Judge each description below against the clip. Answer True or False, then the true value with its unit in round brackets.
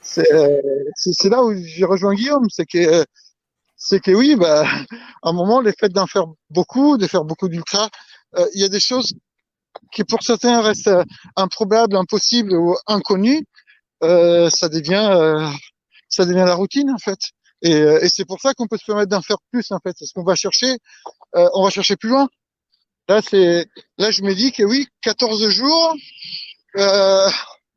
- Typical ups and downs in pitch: True (4.6 semitones)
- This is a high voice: True (200 Hz)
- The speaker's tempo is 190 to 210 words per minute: False (180 wpm)